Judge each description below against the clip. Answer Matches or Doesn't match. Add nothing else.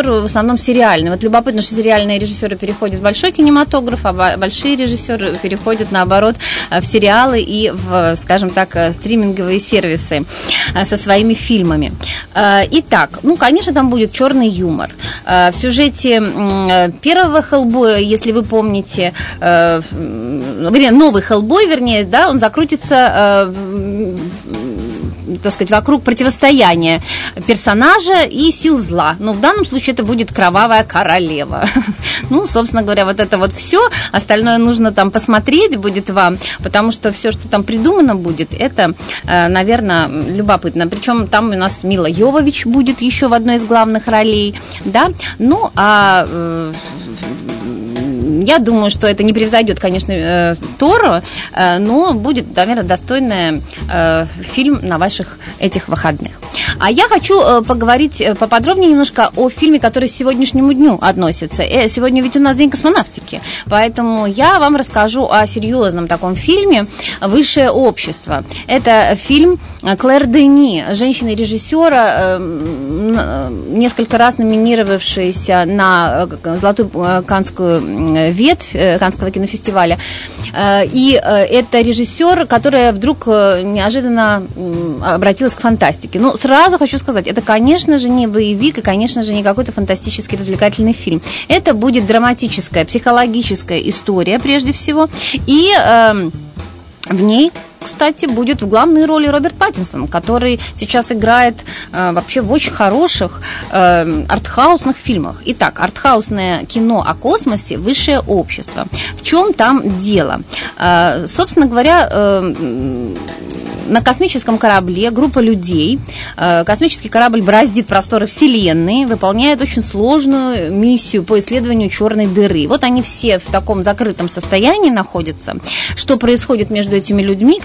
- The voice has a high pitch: Matches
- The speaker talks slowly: Doesn't match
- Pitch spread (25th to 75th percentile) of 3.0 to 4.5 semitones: Doesn't match